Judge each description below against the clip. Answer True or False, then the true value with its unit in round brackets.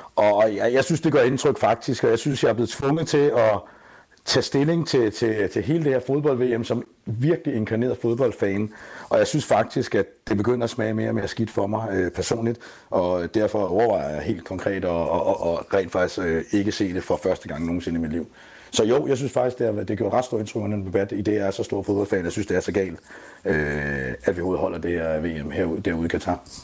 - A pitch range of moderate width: False (5.9 semitones)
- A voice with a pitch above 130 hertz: False (105 Hz)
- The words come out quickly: True (235 wpm)